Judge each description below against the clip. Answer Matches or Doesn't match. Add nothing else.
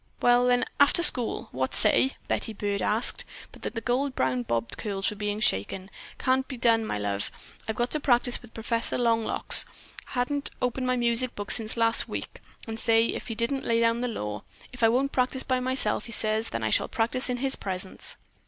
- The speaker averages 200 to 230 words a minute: Matches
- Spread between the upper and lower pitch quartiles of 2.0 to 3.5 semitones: Matches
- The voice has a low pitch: Doesn't match